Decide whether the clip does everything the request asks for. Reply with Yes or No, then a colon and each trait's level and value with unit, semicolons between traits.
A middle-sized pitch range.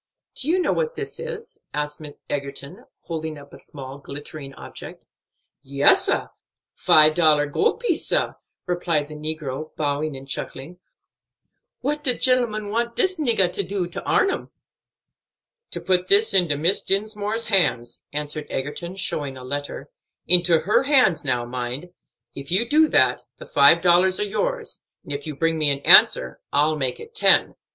No: wide, 6.9 semitones